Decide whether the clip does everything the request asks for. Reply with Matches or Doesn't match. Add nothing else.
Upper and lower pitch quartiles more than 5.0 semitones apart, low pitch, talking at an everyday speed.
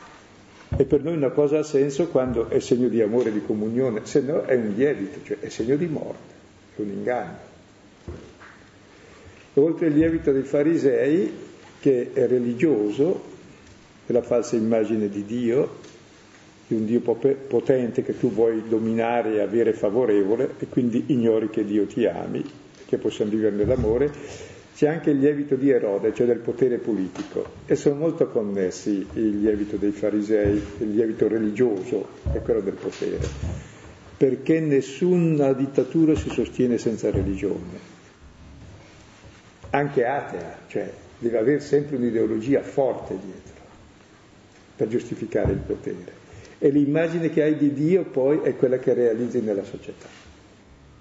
Matches